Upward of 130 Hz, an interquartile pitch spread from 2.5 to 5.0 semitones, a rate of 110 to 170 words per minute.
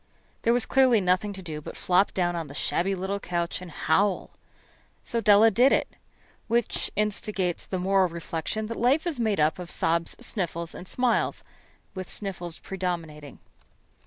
Yes: high, 190 Hz; average, 4.0 semitones; average, 160 wpm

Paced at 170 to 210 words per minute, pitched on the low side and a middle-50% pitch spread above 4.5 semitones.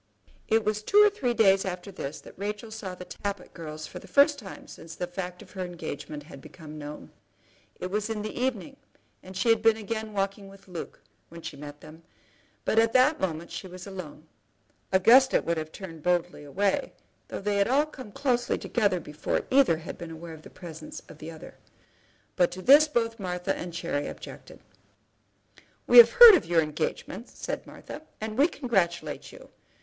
No: average, 190 wpm; high, 190 Hz; average, 5.2 semitones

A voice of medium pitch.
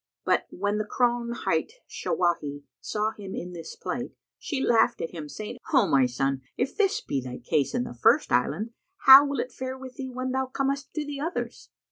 No: high, 230 Hz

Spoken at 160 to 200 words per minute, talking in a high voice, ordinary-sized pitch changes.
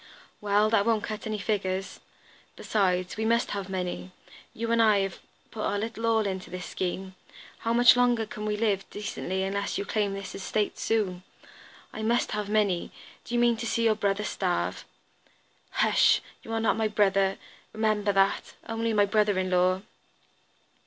No: average, 175 wpm; high, 210 Hz; narrow, 2.3 semitones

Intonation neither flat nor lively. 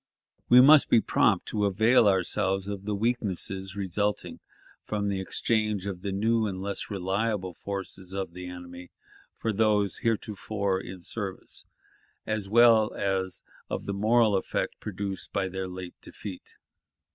No: narrow, 2.3 semitones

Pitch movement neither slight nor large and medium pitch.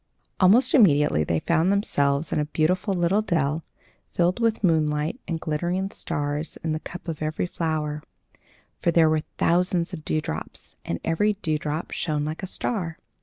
Yes: average, 3.1 semitones; medium, 165 Hz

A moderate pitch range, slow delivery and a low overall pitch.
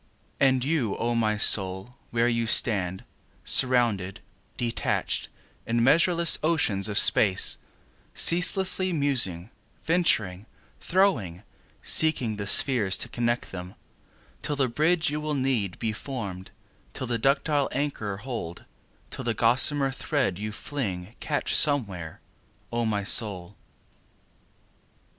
No: wide, 6.1 semitones; slow, 100 wpm; low, 120 Hz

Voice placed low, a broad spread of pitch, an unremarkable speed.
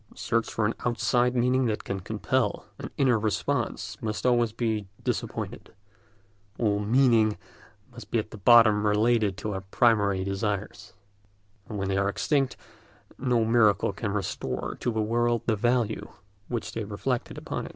No: low, 110 Hz; narrow, 2.6 semitones; average, 155 wpm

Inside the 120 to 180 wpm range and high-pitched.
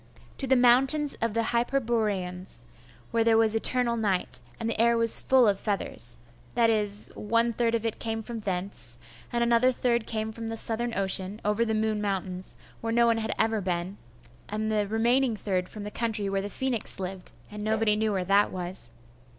No: average, 190 wpm; high, 220 Hz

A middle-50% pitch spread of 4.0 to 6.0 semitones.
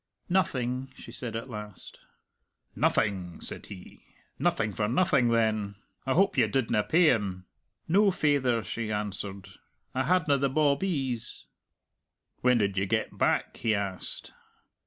Yes: average, 5.1 semitones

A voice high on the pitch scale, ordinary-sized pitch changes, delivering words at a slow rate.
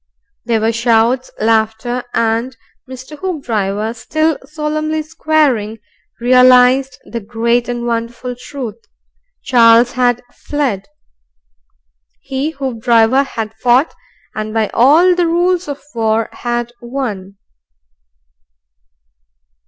Yes: high, 245 Hz; average, 3.5 semitones; slow, 100 wpm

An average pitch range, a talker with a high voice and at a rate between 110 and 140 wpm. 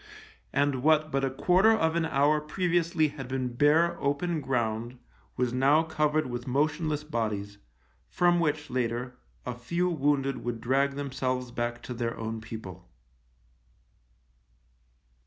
No: average, 4.3 semitones; medium, 140 Hz; slow, 135 wpm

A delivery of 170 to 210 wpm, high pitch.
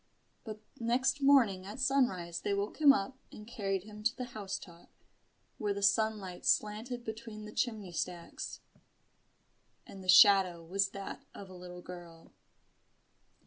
No: average, 145 wpm; high, 205 Hz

